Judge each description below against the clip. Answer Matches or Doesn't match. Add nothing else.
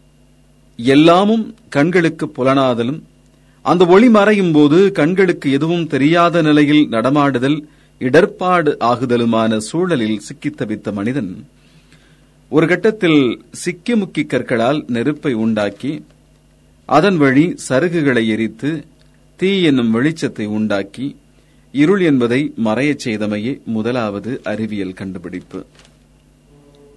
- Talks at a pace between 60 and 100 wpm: Matches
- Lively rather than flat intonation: Matches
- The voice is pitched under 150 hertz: Matches